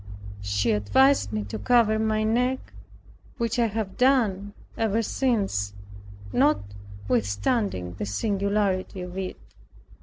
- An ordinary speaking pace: No, slow, 110 wpm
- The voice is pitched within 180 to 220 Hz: Yes, high, 190 Hz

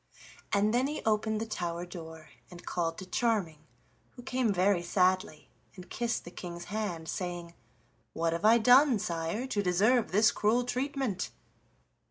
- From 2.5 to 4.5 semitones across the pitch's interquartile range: No, average, 5.0 semitones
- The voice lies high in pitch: Yes, high, 200 Hz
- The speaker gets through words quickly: No, average, 155 wpm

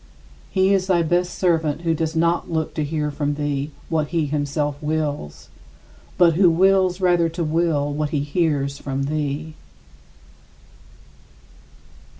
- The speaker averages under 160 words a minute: Yes, average, 140 wpm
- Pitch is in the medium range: Yes, medium, 155 Hz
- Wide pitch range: No, average, 2.8 semitones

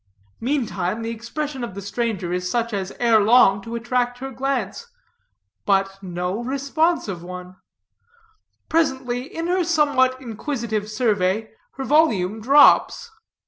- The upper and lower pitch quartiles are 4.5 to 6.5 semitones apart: Yes, average, 5.2 semitones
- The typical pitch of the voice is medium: No, high, 235 Hz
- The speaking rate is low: Yes, slow, 125 wpm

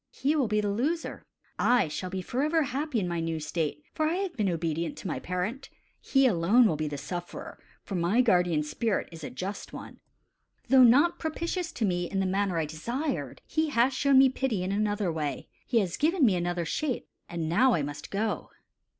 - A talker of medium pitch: No, high, 205 Hz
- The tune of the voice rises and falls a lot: Yes, wide, 7.6 semitones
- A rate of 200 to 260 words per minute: Yes, fast, 205 wpm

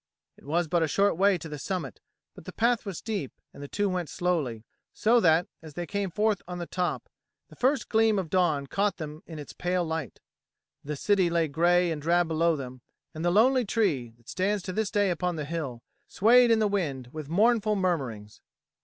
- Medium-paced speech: No, fast, 210 wpm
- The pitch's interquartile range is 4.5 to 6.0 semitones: Yes, average, 4.8 semitones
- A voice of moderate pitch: Yes, medium, 175 Hz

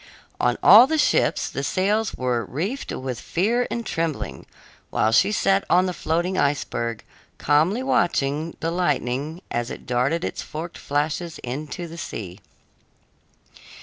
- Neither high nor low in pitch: Yes, medium, 160 Hz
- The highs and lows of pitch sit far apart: Yes, wide, 6.0 semitones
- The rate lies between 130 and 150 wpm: Yes, average, 140 wpm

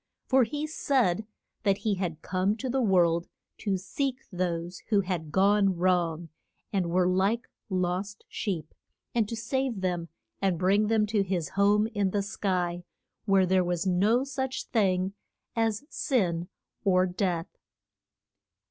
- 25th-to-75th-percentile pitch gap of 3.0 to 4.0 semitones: Yes, average, 3.3 semitones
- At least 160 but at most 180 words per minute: No, average, 145 wpm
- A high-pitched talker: Yes, high, 195 Hz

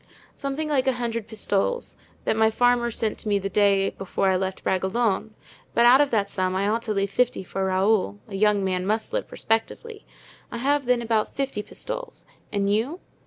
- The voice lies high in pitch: Yes, high, 220 Hz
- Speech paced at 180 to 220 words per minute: Yes, average, 190 wpm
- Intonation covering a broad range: No, average, 3.8 semitones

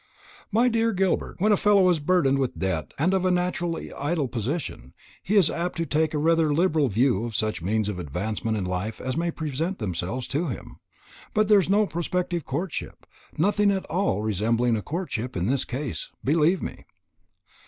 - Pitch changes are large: Yes, wide, 8.2 semitones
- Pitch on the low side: No, medium, 150 Hz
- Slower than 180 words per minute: No, average, 185 wpm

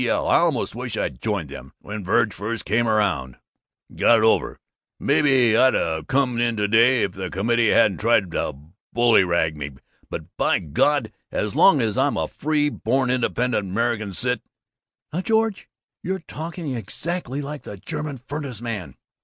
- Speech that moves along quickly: No, average, 170 wpm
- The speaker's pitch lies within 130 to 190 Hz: No, low, 115 Hz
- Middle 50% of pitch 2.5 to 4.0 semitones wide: No, average, 5.1 semitones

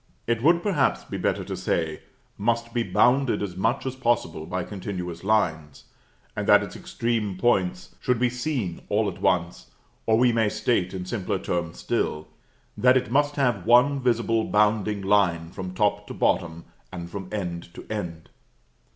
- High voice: No, low, 105 Hz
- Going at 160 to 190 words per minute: Yes, average, 170 wpm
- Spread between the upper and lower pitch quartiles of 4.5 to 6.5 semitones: Yes, average, 5.1 semitones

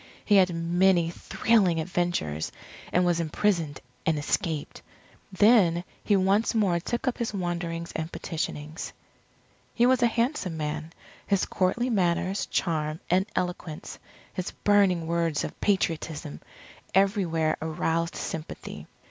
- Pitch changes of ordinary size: Yes, average, 3.4 semitones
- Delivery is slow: Yes, slow, 120 wpm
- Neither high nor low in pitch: Yes, medium, 175 Hz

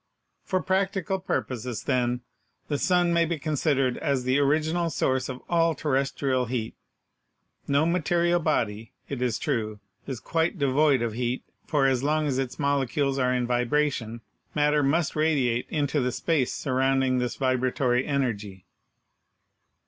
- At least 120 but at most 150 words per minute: Yes, average, 140 wpm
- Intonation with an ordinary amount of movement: Yes, average, 3.6 semitones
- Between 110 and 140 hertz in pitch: Yes, low, 135 Hz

